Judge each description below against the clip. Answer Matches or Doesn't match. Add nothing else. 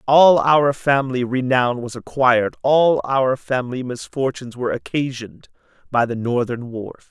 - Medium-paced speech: Doesn't match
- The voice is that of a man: Matches